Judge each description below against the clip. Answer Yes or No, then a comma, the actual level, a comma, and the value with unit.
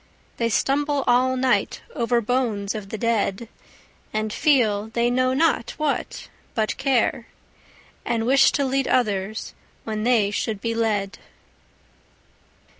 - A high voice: Yes, high, 235 Hz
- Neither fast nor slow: No, slow, 120 wpm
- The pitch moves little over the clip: No, average, 3.2 semitones